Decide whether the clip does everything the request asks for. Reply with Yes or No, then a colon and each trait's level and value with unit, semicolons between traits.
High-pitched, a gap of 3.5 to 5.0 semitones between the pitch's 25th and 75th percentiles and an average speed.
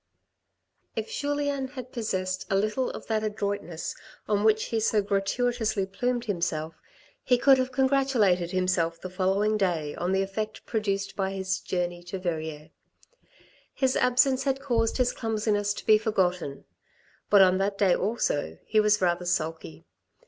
Yes: high, 205 Hz; average, 4.3 semitones; average, 150 wpm